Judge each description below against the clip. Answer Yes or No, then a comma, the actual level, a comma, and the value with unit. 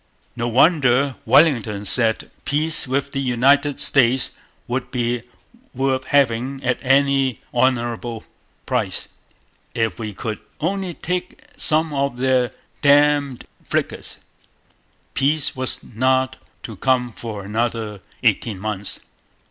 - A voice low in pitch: Yes, low, 130 Hz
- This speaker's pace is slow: Yes, slow, 110 wpm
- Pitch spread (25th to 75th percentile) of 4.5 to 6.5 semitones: No, average, 3.1 semitones